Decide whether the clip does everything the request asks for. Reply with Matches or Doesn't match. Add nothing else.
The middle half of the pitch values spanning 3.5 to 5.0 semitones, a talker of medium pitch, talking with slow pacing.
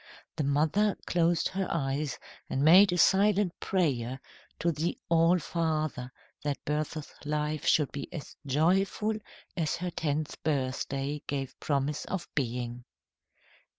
Matches